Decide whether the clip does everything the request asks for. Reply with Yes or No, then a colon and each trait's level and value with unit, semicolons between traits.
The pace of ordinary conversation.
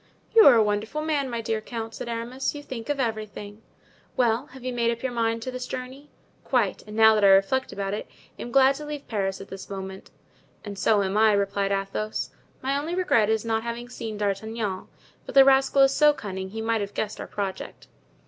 No: fast, 220 wpm